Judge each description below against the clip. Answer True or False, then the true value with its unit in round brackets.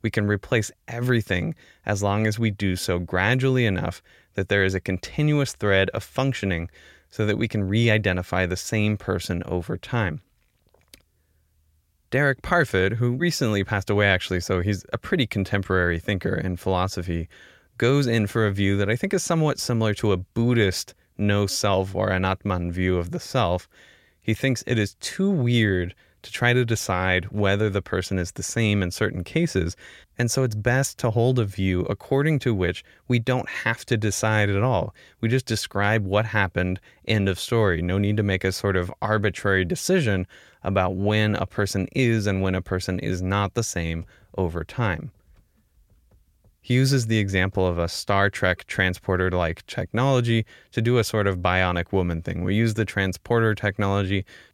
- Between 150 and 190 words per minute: True (180 wpm)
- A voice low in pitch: True (100 Hz)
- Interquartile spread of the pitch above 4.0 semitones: False (3.7 semitones)